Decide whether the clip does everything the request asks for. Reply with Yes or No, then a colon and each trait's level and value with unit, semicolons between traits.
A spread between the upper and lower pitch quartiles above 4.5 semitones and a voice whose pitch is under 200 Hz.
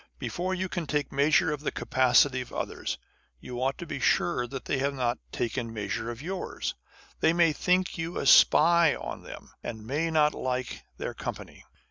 Yes: average, 4.9 semitones; medium, 140 Hz